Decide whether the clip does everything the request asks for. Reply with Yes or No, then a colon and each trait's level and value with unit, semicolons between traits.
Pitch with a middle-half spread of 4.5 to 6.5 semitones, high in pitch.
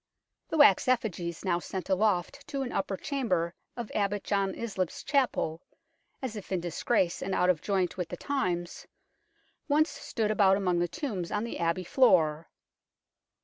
Yes: average, 5.0 semitones; high, 195 Hz